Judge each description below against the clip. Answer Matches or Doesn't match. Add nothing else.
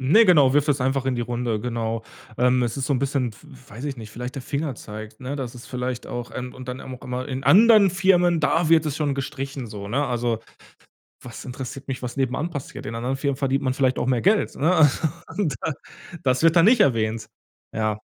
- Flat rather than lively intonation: Doesn't match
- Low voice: Matches